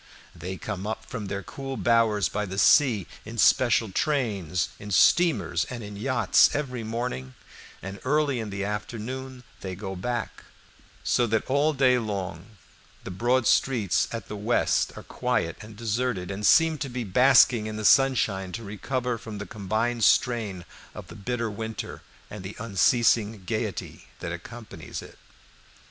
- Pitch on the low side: Yes, low, 110 Hz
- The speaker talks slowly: No, average, 160 wpm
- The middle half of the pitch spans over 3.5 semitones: Yes, average, 3.9 semitones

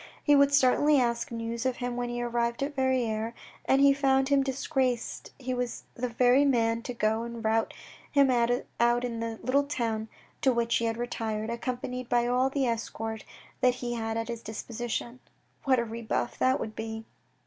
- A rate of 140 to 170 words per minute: No, average, 190 wpm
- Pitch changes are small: Yes, narrow, 2.1 semitones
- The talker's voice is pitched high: Yes, high, 240 Hz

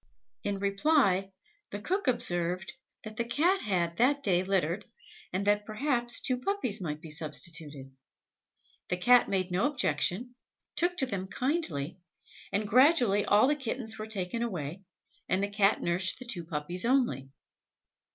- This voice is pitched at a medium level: No, high, 205 Hz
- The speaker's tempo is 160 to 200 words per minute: No, average, 150 wpm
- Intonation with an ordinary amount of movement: No, wide, 5.8 semitones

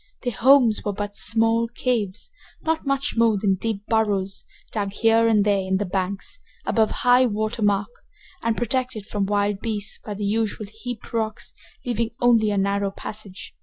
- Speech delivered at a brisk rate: No, average, 165 wpm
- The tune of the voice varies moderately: No, narrow, 2.3 semitones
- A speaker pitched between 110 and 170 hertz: No, high, 215 Hz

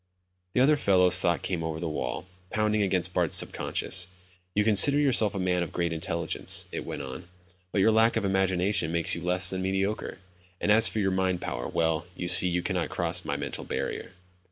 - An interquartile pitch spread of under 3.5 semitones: Yes, average, 3.0 semitones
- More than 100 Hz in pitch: No, very low, 90 Hz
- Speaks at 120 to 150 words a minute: No, fast, 205 wpm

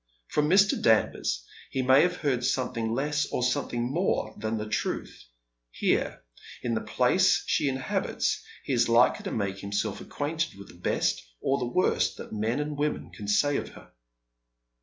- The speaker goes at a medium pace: Yes, average, 170 wpm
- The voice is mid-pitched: No, low, 125 Hz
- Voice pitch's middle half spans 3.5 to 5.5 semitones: Yes, average, 4.9 semitones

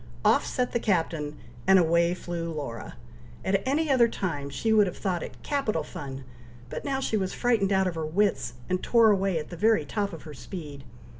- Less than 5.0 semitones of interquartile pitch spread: No, average, 5.3 semitones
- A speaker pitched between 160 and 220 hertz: Yes, medium, 185 Hz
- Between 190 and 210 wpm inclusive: Yes, fast, 205 wpm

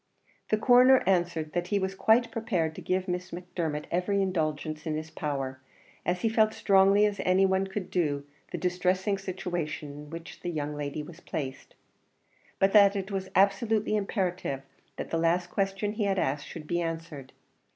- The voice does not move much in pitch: No, average, 3.8 semitones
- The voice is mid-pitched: Yes, medium, 180 Hz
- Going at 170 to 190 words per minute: Yes, average, 180 wpm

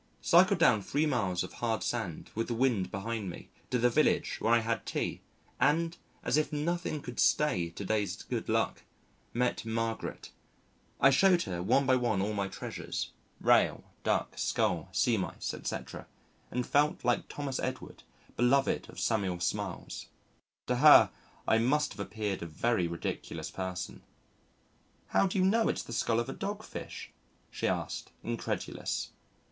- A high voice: No, low, 115 Hz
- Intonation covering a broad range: Yes, wide, 5.7 semitones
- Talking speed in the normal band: Yes, average, 160 wpm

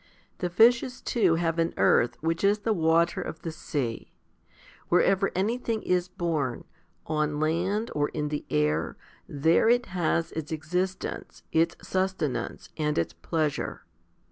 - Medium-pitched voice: Yes, medium, 165 Hz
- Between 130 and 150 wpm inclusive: Yes, average, 140 wpm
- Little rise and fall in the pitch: No, average, 3.7 semitones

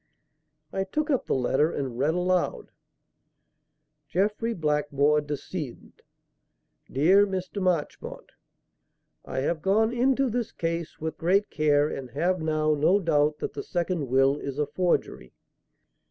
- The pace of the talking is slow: Yes, slow, 130 wpm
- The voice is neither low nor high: Yes, medium, 160 Hz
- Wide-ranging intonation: No, average, 4.5 semitones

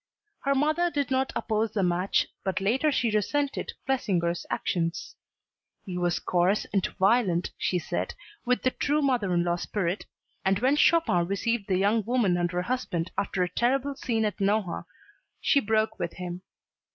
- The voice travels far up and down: Yes, wide, 6.1 semitones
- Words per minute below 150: No, average, 165 wpm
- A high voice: Yes, high, 210 Hz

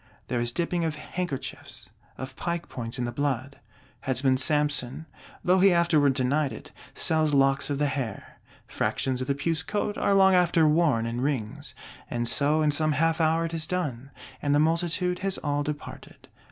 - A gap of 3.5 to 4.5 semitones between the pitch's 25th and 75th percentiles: Yes, average, 4.1 semitones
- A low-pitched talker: No, medium, 150 Hz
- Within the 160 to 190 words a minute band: Yes, average, 180 wpm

